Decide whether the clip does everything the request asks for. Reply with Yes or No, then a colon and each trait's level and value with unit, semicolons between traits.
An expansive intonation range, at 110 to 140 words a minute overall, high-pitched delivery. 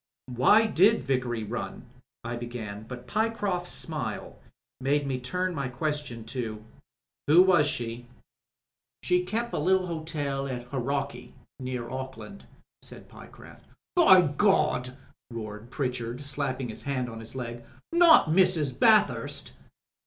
No: wide, 6.4 semitones; slow, 135 wpm; low, 135 Hz